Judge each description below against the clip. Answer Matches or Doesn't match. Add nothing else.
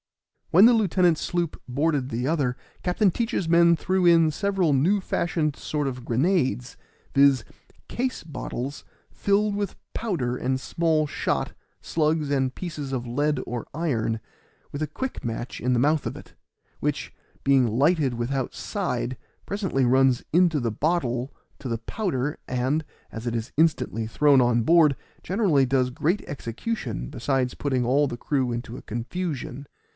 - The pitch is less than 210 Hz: Matches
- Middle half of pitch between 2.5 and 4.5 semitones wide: Doesn't match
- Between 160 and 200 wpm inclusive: Doesn't match